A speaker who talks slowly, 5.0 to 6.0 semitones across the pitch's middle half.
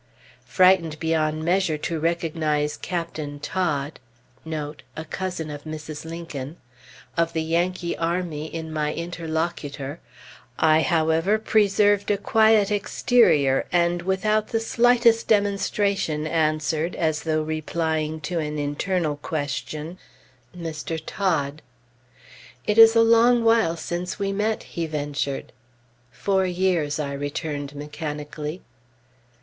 No: slow, 100 wpm; average, 3.8 semitones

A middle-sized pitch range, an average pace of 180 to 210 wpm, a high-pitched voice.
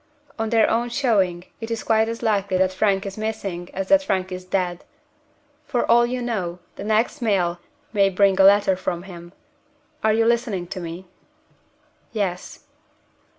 No: average, 3.5 semitones; average, 165 wpm; high, 200 Hz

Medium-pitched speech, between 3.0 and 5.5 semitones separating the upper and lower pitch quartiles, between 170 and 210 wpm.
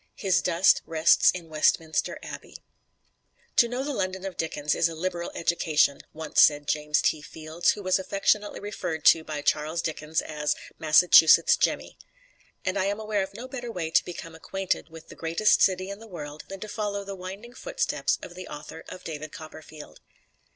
Yes: medium, 170 Hz; average, 3.9 semitones; average, 180 wpm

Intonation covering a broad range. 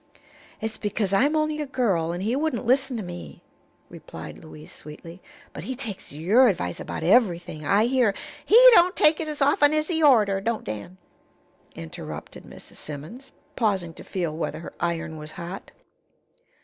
Yes: wide, 7.9 semitones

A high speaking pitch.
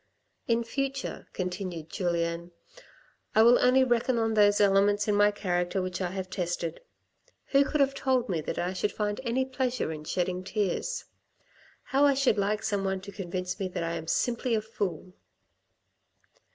Yes: high, 205 Hz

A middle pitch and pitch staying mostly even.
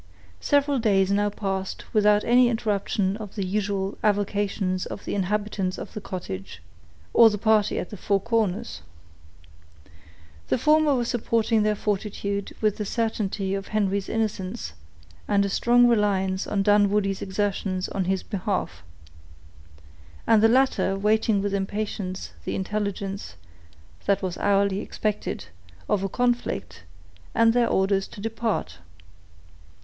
No: high, 205 Hz; narrow, 2.2 semitones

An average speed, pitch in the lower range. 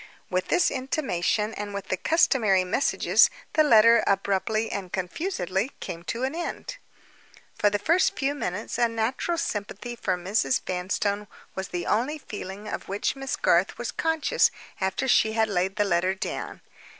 No: average, 160 wpm; high, 210 Hz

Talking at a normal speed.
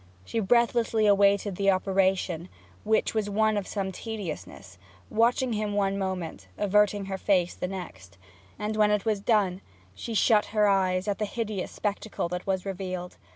Yes: average, 160 wpm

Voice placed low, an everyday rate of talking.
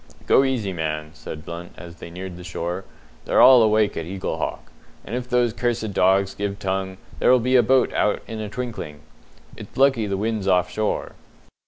Yes: low, 100 Hz; average, 185 wpm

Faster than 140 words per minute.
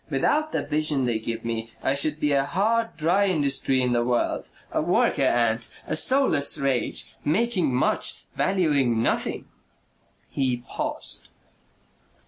No: slow, 135 wpm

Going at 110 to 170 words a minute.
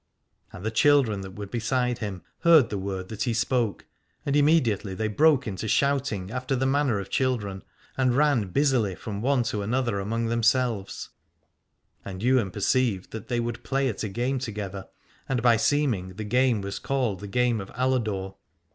No: average, 180 wpm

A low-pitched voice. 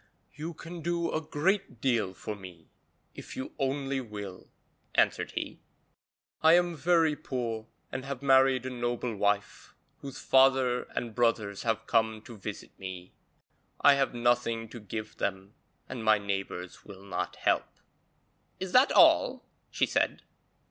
Yes: low, 120 Hz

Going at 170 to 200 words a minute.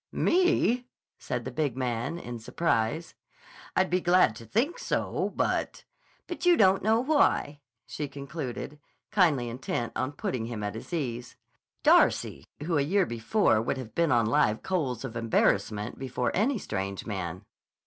No: average, 155 wpm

